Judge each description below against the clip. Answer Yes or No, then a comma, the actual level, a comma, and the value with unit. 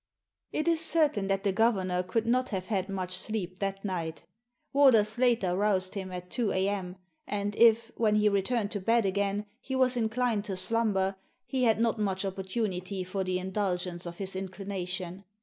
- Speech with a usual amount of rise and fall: Yes, average, 3.4 semitones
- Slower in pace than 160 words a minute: No, average, 180 wpm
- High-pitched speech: Yes, high, 200 Hz